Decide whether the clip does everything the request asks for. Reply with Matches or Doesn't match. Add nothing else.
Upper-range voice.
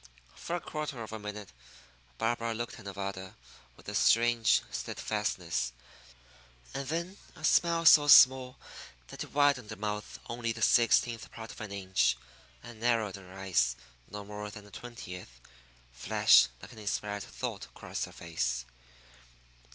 Doesn't match